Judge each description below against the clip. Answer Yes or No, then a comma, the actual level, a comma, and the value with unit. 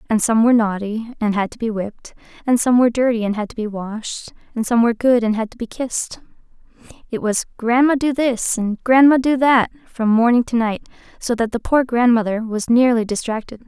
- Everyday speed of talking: No, fast, 210 wpm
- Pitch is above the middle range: Yes, high, 230 Hz